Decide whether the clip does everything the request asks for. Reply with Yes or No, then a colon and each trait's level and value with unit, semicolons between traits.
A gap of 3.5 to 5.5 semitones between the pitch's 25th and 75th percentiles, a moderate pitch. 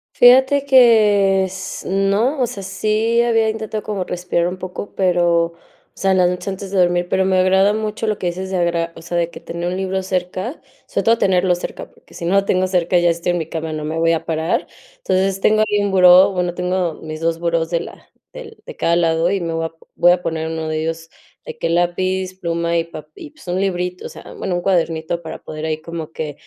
No: average, 2.7 semitones; medium, 180 Hz